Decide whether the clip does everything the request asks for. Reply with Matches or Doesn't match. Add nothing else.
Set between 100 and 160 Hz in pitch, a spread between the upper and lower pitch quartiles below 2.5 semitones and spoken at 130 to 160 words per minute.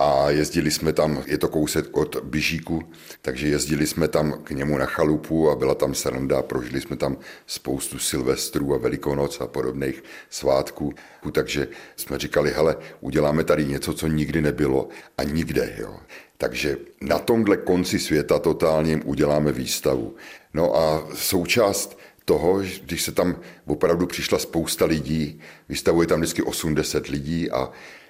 Doesn't match